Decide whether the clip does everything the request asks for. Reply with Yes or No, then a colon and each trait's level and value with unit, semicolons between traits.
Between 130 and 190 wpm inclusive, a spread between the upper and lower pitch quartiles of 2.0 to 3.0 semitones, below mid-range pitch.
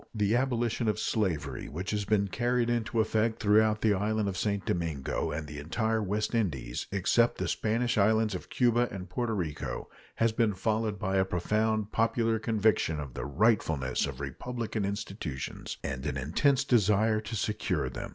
No: average, 170 wpm; average, 3.7 semitones; low, 105 Hz